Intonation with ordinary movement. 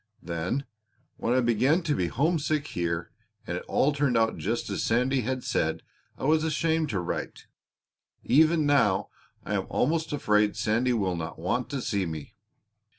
No: wide, 6.5 semitones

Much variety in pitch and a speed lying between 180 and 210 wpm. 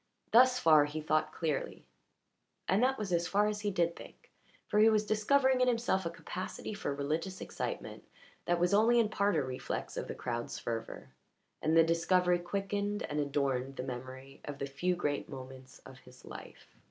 Yes: wide, 6.7 semitones; average, 185 wpm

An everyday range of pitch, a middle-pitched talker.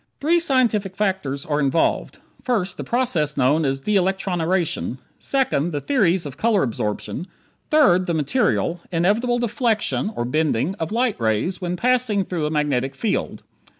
No: wide, 7.2 semitones; medium, 180 Hz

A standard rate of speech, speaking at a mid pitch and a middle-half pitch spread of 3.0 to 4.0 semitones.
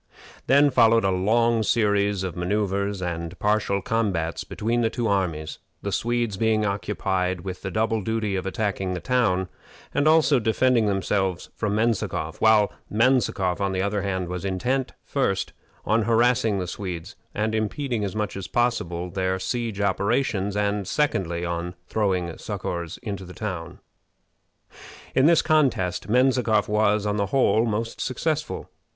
No: average, 150 wpm; low, 105 Hz; average, 3.5 semitones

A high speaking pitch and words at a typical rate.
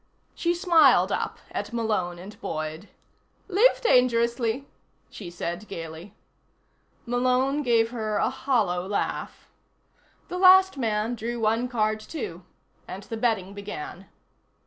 No: high, 225 Hz; slow, 120 wpm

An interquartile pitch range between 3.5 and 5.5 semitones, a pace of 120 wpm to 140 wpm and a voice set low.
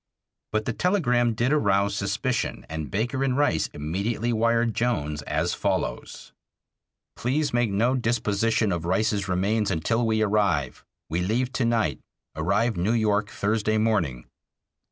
Yes: average, 3.9 semitones; slow, 135 wpm; low, 110 Hz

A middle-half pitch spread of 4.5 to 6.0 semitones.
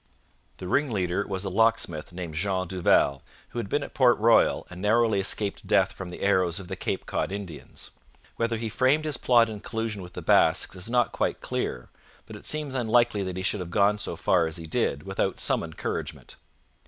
No: average, 4.1 semitones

